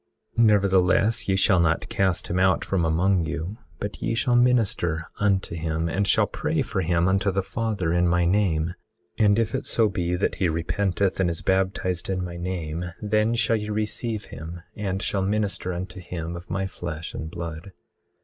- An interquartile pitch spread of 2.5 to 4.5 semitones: Yes, average, 3.1 semitones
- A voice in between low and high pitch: No, very low, 95 Hz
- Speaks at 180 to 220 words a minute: Yes, average, 190 wpm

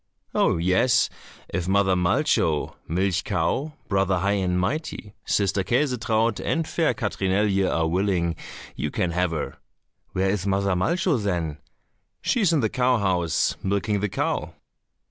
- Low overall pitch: Yes, low, 100 Hz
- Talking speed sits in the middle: Yes, average, 145 wpm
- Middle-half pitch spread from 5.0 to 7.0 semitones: No, average, 3.6 semitones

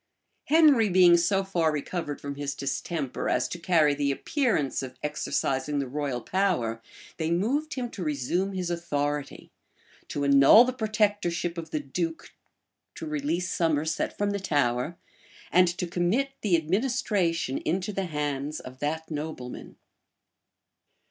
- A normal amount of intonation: Yes, average, 4.8 semitones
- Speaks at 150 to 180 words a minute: No, average, 140 wpm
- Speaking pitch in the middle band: Yes, medium, 165 Hz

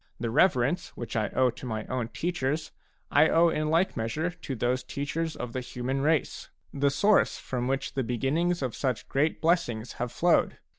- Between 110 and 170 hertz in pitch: Yes, low, 135 Hz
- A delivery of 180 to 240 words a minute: Yes, average, 185 wpm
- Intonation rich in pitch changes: No, average, 4.8 semitones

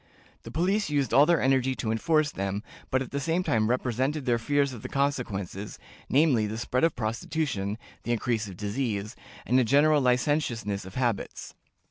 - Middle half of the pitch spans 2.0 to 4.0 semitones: No, average, 4.8 semitones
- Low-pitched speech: Yes, low, 125 Hz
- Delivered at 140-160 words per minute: No, average, 175 wpm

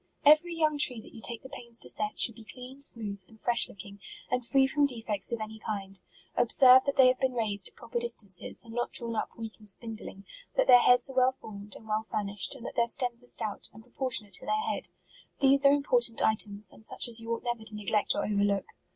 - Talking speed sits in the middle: No, fast, 235 wpm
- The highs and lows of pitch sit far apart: No, average, 3.1 semitones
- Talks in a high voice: Yes, high, 230 Hz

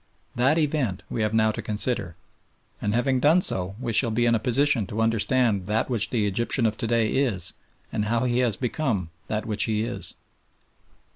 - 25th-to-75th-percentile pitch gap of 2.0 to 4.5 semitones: Yes, average, 2.9 semitones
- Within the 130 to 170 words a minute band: No, average, 195 wpm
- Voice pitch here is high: No, low, 115 Hz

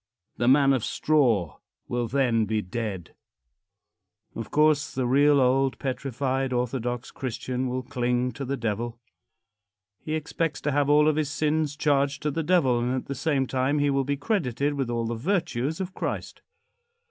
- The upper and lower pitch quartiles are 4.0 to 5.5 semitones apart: No, average, 3.1 semitones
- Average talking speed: Yes, average, 170 wpm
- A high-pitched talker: No, low, 135 Hz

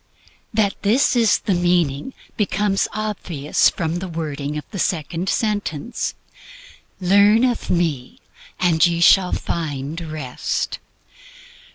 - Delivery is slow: Yes, slow, 110 wpm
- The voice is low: No, medium, 175 Hz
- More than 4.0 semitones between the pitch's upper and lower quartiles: Yes, average, 4.6 semitones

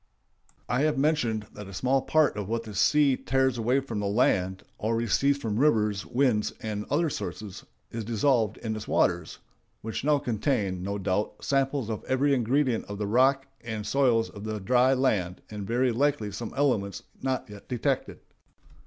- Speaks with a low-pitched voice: Yes, low, 115 Hz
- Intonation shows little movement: No, average, 4.3 semitones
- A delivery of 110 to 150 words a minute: No, average, 175 wpm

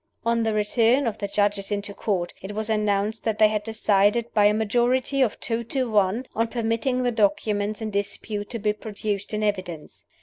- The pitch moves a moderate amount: No, narrow, 1.9 semitones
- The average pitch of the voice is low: No, high, 215 Hz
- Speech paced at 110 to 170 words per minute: No, average, 195 wpm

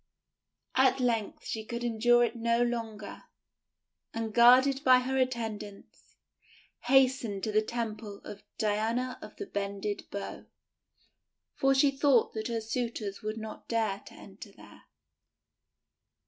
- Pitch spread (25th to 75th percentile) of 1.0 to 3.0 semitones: Yes, average, 2.7 semitones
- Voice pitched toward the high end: Yes, high, 230 Hz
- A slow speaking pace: Yes, slow, 130 wpm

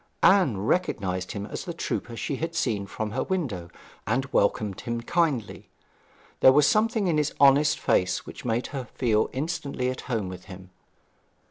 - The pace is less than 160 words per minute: No, average, 165 wpm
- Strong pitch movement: Yes, wide, 6.6 semitones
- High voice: No, low, 125 Hz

